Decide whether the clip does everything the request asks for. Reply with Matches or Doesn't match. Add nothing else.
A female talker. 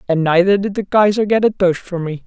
Matches